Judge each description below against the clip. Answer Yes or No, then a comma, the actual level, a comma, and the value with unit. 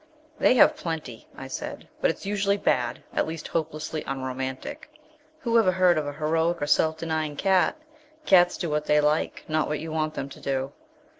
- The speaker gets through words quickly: No, average, 190 wpm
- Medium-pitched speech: Yes, medium, 155 Hz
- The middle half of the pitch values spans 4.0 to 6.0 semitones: No, average, 3.0 semitones